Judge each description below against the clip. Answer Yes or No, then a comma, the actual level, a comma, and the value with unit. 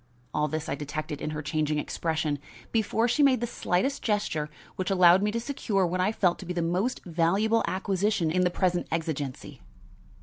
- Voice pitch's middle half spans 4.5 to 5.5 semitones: Yes, average, 4.9 semitones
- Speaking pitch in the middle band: Yes, medium, 180 Hz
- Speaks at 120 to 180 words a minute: No, average, 190 wpm